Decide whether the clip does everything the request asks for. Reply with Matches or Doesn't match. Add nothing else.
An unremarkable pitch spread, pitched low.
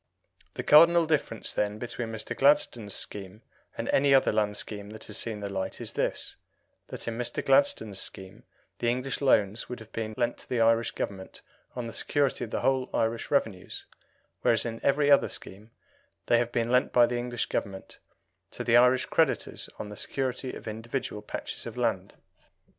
Matches